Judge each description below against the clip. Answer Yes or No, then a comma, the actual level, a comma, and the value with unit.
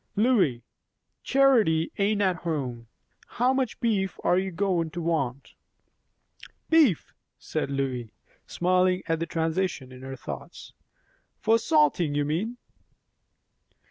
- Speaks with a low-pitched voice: No, medium, 170 Hz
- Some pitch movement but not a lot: No, wide, 5.8 semitones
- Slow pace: Yes, slow, 115 wpm